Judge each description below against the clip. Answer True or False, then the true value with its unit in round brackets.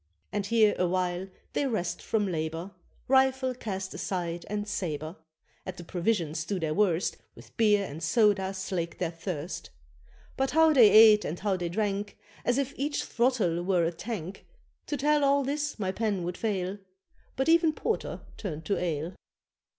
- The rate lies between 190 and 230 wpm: False (165 wpm)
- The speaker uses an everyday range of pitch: True (5.0 semitones)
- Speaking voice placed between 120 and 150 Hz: False (195 Hz)